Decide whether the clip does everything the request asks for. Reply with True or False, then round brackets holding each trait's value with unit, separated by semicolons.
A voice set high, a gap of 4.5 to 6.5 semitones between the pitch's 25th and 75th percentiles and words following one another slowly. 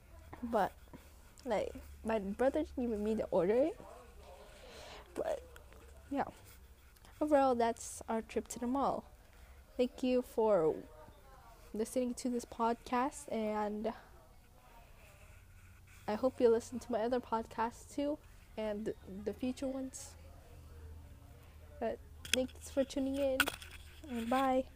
False (235 Hz; 3.9 semitones; 115 wpm)